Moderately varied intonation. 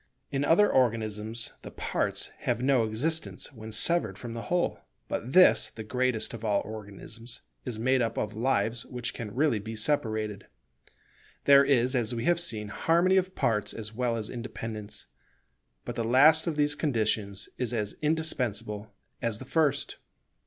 Yes: average, 4.3 semitones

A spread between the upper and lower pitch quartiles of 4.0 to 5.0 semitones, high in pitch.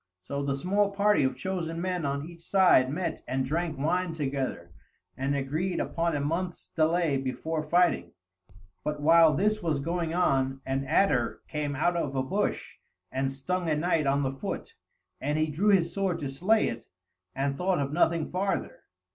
No: average, 4.5 semitones; medium, 160 Hz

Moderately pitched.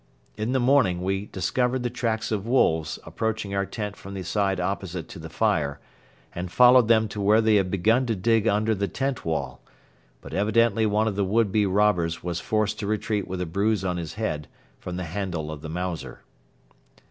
No: low, 100 Hz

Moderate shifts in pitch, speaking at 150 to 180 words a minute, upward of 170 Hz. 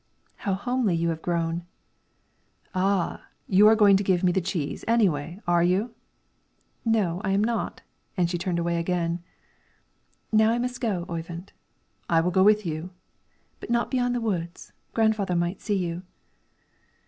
Yes: average, 4.0 semitones; average, 160 wpm; medium, 185 Hz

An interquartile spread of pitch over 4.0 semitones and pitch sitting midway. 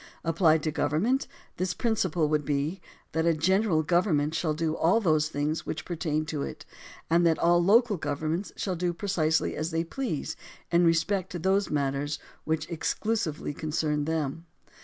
No: average, 2.8 semitones; medium, 160 Hz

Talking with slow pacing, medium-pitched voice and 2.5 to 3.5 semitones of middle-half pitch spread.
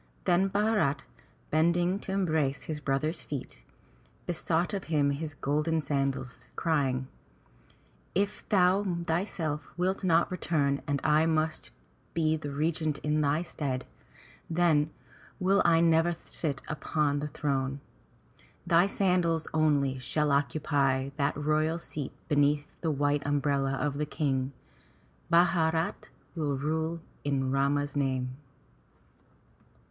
Yes: slow, 120 wpm; medium, 150 Hz; average, 2.9 semitones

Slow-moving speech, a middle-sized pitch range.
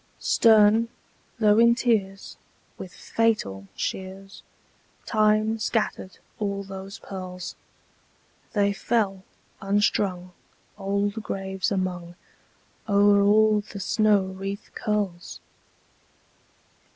No: slow, 85 wpm; narrow, 1.9 semitones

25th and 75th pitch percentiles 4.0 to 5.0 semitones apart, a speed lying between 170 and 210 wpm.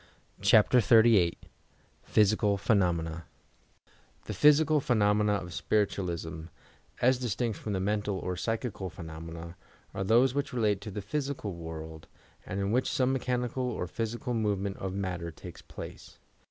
No: average, 4.7 semitones; average, 140 wpm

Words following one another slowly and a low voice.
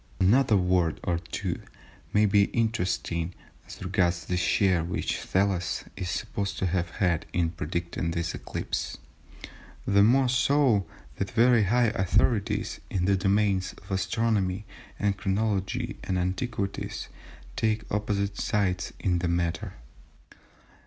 Yes: slow, 125 wpm; very low, 95 Hz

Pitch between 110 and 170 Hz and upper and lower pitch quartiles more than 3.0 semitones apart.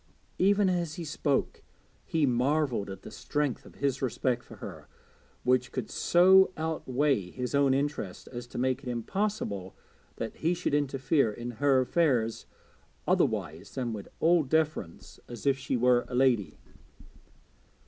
Yes: low, 135 Hz; average, 4.3 semitones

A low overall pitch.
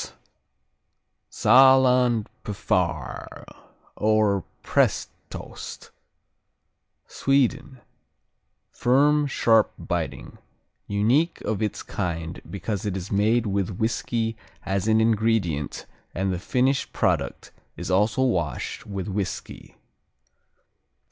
Yes: low, 110 Hz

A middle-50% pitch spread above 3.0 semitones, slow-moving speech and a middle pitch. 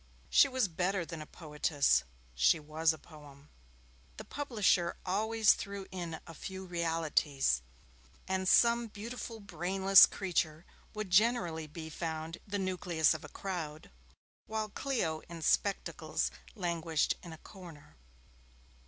Yes: average, 4.0 semitones; slow, 125 wpm; medium, 175 Hz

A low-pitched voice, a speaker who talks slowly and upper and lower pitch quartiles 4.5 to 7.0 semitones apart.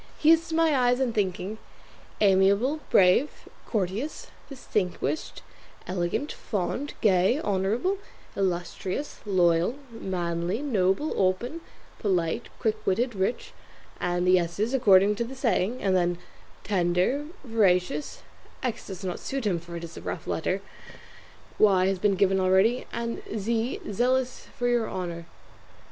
No: high, 200 Hz; slow, 130 wpm; average, 5.1 semitones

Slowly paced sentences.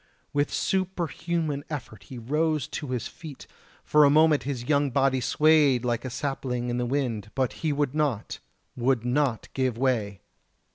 No: average, 165 wpm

